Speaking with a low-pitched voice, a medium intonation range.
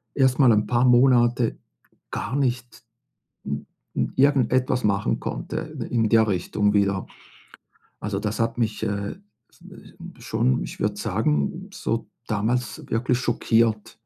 Yes: low, 115 Hz; average, 3.1 semitones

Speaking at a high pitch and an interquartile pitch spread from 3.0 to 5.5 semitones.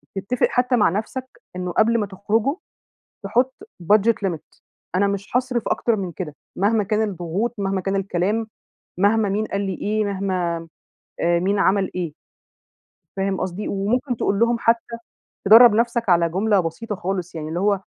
Yes: high, 200 Hz; average, 3.3 semitones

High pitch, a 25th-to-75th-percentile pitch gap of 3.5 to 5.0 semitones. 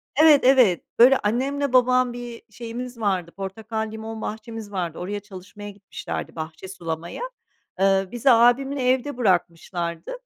Yes: high, 220 Hz; average, 4.7 semitones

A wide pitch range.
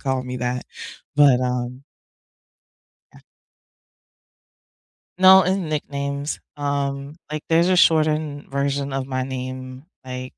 No: average, 2.8 semitones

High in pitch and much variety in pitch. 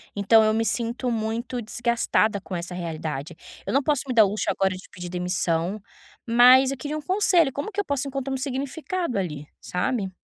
Yes: high, 230 Hz; wide, 6.4 semitones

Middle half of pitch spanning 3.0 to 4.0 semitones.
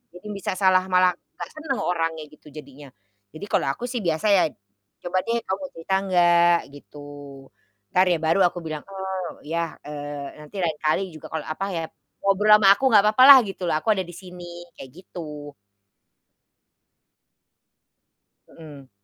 Yes: average, 3.6 semitones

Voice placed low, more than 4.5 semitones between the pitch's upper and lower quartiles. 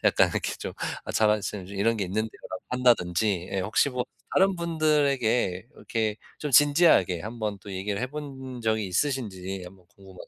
Yes: low, 110 Hz; wide, 5.5 semitones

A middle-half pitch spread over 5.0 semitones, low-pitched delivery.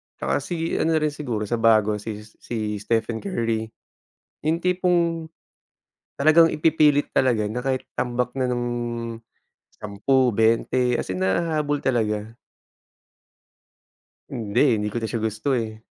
Yes: wide, 5.4 semitones; low, 120 Hz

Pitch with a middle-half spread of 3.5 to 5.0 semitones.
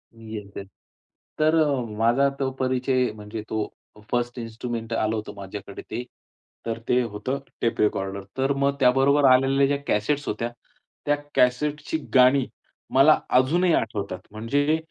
Yes: average, 4.0 semitones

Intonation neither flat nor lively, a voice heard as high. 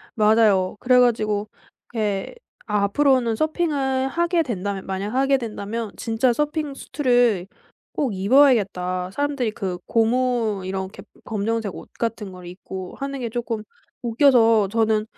Yes: average, 4.4 semitones; high, 225 Hz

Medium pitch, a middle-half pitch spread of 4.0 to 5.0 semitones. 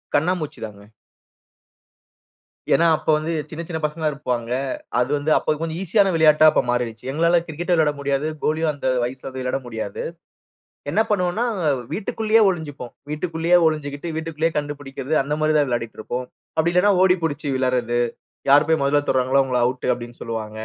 Yes: medium, 150 Hz; average, 4.3 semitones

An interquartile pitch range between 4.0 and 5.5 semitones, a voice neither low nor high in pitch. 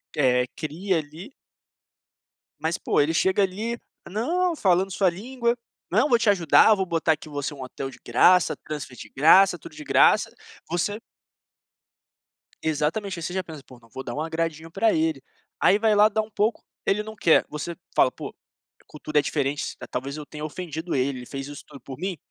Yes: average, 5.2 semitones; medium, 165 Hz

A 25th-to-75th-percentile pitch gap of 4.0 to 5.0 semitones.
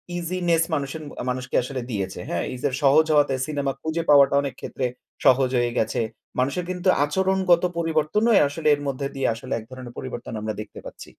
Yes: average, 4.4 semitones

